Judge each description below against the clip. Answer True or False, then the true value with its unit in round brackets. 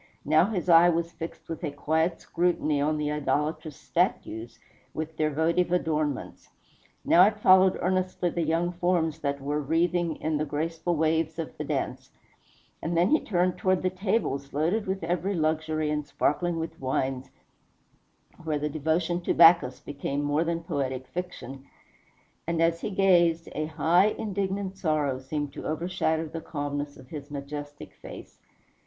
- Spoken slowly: False (160 wpm)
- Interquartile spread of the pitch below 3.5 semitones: True (3.0 semitones)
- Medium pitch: True (160 Hz)